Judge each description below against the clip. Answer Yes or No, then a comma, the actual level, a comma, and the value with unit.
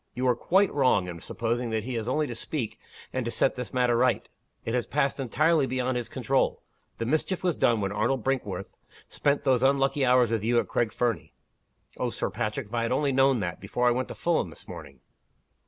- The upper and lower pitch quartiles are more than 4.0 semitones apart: No, average, 2.9 semitones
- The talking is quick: Yes, fast, 220 wpm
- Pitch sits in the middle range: No, low, 125 Hz